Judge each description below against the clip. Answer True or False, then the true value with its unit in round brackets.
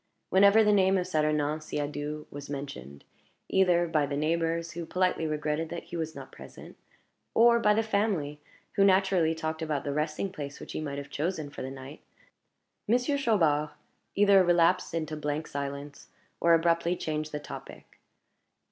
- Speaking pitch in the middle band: True (160 Hz)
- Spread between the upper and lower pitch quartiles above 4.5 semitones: False (3.9 semitones)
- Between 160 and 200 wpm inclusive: True (165 wpm)